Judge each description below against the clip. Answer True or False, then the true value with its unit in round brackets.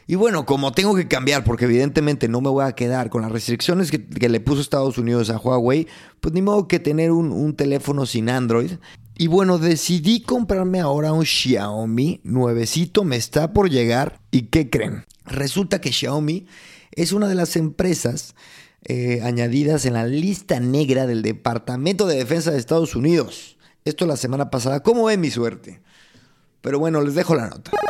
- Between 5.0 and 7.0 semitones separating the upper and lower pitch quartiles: True (5.5 semitones)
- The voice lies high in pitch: False (145 Hz)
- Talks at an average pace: True (180 wpm)